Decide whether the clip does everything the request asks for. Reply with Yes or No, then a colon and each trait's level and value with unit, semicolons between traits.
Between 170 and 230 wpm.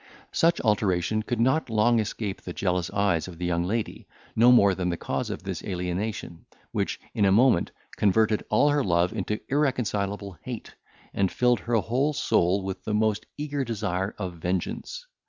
Yes: average, 175 wpm